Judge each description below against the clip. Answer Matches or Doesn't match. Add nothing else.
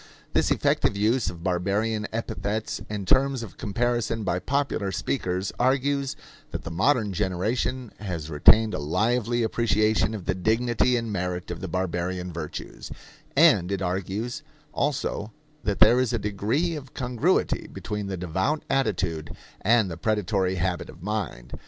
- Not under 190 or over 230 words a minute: Doesn't match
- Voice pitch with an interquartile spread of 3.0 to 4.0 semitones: Doesn't match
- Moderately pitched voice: Doesn't match